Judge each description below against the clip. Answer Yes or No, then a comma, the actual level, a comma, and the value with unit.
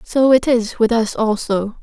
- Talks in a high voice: Yes, high, 230 Hz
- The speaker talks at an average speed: Yes, average, 195 wpm